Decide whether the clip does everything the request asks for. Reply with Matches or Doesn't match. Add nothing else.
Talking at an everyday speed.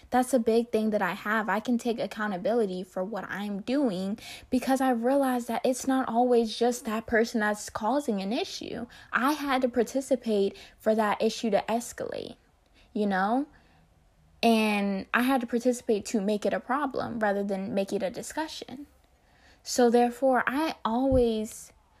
Matches